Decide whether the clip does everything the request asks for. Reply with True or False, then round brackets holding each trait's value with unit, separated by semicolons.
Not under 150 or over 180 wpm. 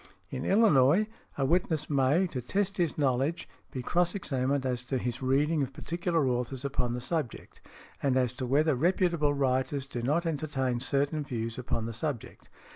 True (170 wpm)